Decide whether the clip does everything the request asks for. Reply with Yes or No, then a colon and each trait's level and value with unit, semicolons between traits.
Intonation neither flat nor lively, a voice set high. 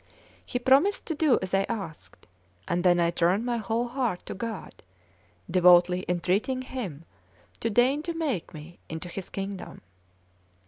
No: wide, 5.9 semitones; high, 195 Hz